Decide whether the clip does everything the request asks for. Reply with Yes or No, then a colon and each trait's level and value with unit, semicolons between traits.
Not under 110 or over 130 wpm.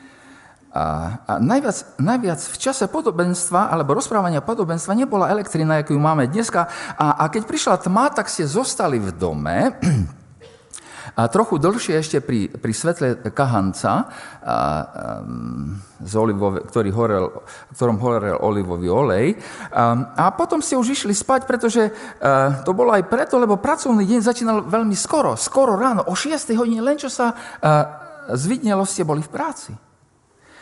No: average, 145 wpm